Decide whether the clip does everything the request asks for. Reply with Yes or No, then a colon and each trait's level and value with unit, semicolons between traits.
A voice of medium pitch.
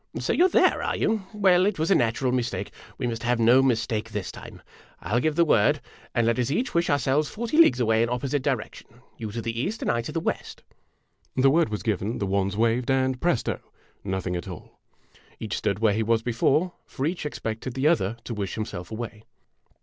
No: low, 120 Hz